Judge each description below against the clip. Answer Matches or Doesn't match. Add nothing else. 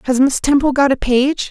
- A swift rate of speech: Matches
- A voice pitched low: Doesn't match